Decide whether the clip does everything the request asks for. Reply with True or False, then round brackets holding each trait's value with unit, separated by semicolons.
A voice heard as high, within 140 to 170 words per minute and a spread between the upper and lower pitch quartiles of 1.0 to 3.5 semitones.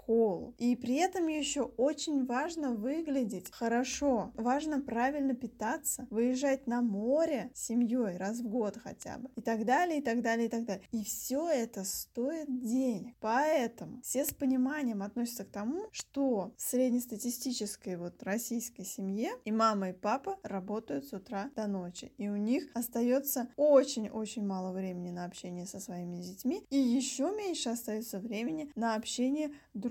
False (240 Hz; 160 wpm; 3.9 semitones)